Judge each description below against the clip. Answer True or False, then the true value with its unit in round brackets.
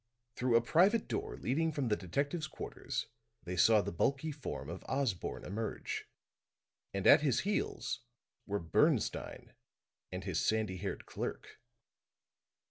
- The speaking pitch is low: True (115 Hz)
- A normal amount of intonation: False (7.0 semitones)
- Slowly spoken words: True (130 wpm)